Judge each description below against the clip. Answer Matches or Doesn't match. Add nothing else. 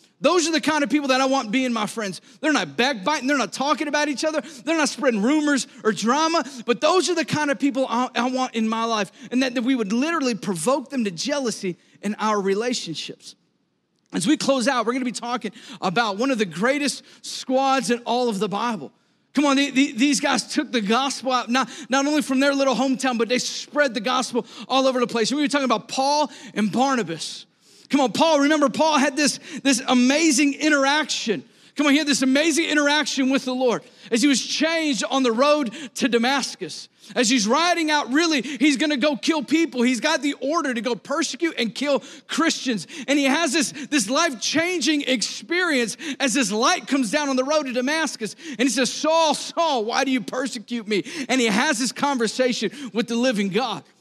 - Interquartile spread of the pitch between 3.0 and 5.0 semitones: Matches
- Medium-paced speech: Doesn't match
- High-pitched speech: Matches